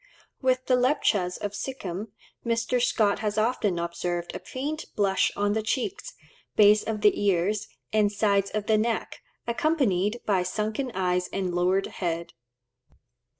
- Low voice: No, high, 210 Hz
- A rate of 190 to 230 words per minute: No, average, 145 wpm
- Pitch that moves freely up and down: No, average, 3.9 semitones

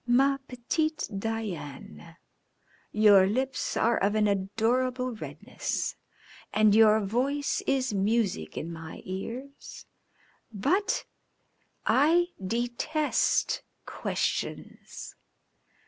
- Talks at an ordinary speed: No, slow, 85 wpm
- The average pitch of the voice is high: Yes, high, 225 Hz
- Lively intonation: No, average, 4.8 semitones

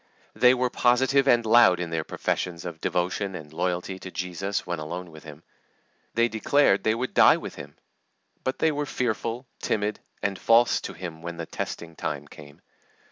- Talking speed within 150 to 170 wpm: No, average, 180 wpm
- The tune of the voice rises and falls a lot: Yes, wide, 5.9 semitones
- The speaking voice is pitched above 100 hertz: No, very low, 95 Hz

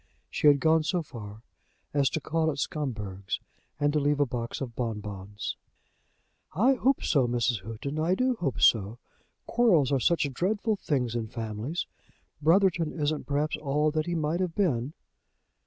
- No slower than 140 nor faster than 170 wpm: Yes, average, 160 wpm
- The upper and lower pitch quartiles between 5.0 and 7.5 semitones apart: Yes, wide, 5.6 semitones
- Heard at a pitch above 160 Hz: No, medium, 145 Hz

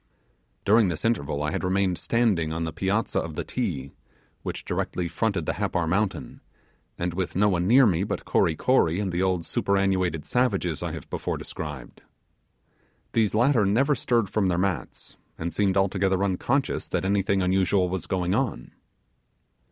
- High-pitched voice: No, very low, 95 Hz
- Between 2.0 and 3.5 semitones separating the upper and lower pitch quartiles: Yes, average, 3.2 semitones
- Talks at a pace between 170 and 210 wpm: No, average, 160 wpm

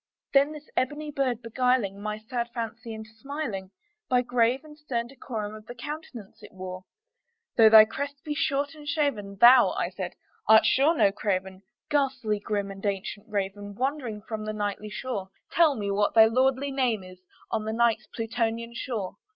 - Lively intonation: No, average, 4.4 semitones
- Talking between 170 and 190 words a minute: Yes, average, 175 wpm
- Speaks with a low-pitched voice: No, high, 230 Hz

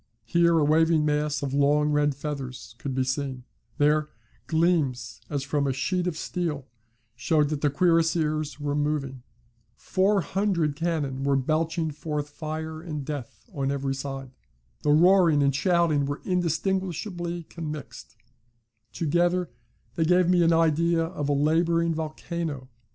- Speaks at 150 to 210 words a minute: No, average, 140 wpm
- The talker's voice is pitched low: No, medium, 155 Hz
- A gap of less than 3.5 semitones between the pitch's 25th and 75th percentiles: Yes, average, 2.9 semitones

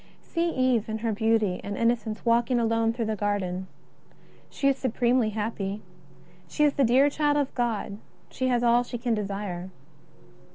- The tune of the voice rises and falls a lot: No, average, 3.1 semitones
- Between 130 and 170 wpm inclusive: Yes, average, 165 wpm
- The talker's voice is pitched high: Yes, high, 230 Hz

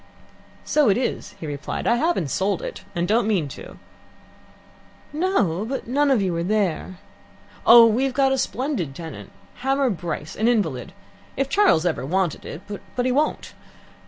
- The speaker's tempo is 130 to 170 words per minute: Yes, average, 160 wpm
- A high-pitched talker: Yes, high, 215 Hz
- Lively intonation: Yes, wide, 7.6 semitones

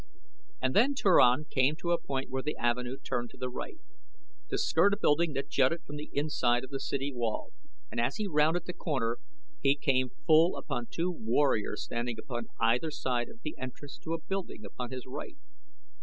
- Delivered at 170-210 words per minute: Yes, average, 195 wpm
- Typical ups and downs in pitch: Yes, average, 4.5 semitones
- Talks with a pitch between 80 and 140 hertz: Yes, low, 135 Hz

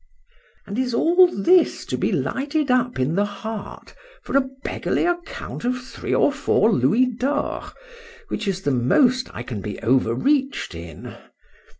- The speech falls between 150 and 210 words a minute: Yes, average, 160 wpm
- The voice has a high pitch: Yes, high, 240 Hz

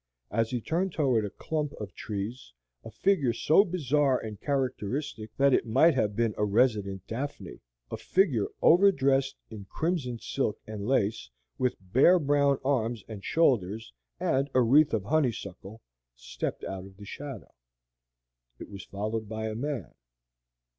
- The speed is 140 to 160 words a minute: Yes, average, 155 wpm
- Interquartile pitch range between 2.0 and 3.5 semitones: No, average, 5.2 semitones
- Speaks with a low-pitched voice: Yes, low, 120 Hz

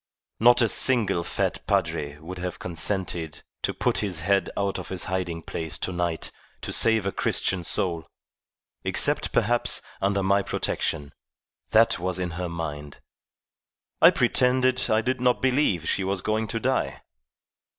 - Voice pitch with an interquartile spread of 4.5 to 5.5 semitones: Yes, average, 4.8 semitones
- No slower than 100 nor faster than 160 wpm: Yes, average, 150 wpm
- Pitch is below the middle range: Yes, very low, 95 Hz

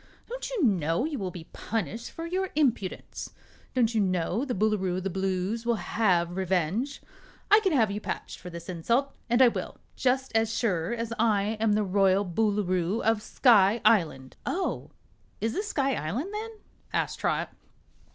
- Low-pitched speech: No, high, 215 Hz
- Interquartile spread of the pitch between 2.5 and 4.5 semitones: No, average, 5.1 semitones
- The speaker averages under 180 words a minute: Yes, average, 170 wpm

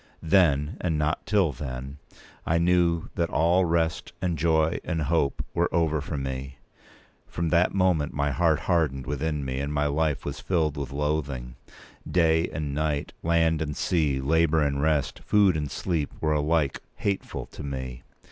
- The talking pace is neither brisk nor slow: Yes, average, 165 wpm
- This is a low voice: Yes, very low, 80 Hz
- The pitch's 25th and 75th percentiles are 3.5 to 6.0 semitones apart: No, average, 2.8 semitones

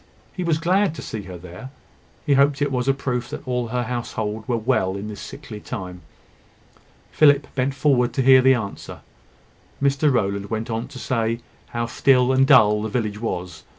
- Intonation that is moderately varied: Yes, average, 4.2 semitones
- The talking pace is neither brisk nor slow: Yes, average, 185 wpm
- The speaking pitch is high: No, low, 125 Hz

